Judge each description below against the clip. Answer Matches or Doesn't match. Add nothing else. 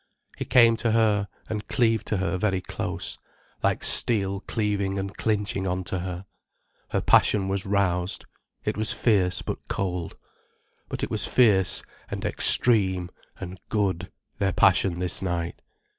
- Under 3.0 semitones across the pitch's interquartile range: Matches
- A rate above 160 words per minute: Doesn't match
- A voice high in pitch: Doesn't match